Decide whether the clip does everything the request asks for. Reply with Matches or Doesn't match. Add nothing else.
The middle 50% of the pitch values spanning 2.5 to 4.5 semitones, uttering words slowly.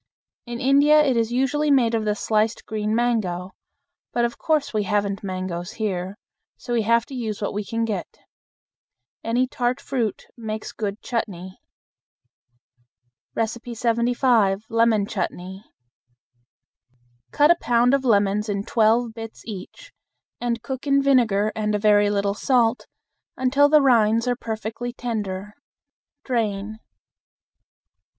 Matches